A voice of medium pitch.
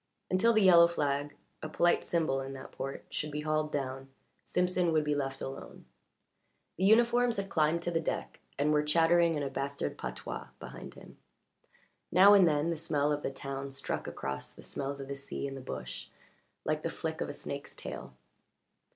Yes: medium, 150 Hz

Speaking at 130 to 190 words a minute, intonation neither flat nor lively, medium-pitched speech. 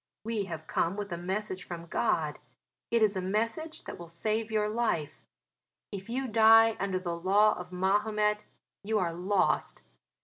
No: average, 165 wpm; average, 3.3 semitones; high, 205 Hz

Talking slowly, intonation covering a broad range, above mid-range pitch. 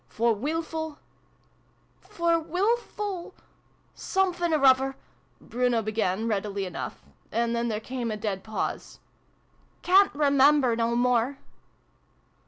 Yes: slow, 110 wpm; wide, 6.1 semitones; very high, 255 Hz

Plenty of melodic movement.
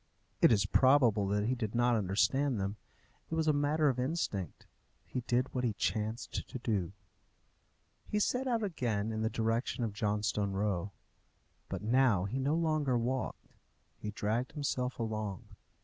No: average, 4.1 semitones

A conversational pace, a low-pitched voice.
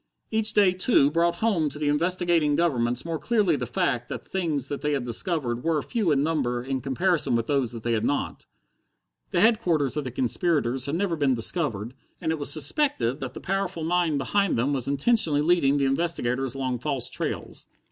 No: average, 190 wpm; medium, 150 Hz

